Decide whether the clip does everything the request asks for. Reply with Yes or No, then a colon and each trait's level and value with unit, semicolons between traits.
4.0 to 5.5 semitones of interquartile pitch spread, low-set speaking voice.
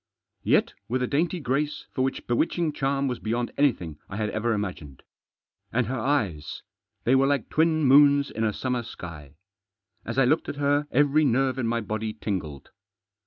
Yes: average, 4.7 semitones; low, 125 Hz